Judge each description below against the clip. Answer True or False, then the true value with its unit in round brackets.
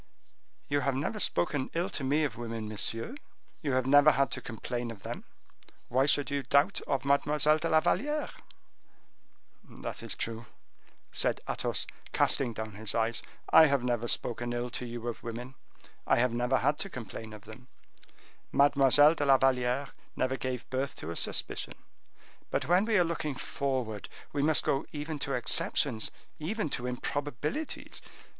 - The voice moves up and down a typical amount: True (3.4 semitones)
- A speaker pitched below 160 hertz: True (135 Hz)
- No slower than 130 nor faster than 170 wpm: True (165 wpm)